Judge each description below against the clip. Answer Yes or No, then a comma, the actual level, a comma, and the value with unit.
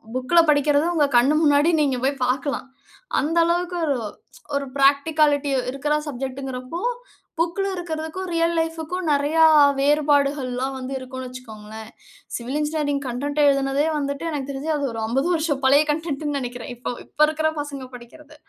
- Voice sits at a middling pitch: No, very high, 285 Hz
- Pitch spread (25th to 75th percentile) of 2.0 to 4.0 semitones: Yes, average, 2.8 semitones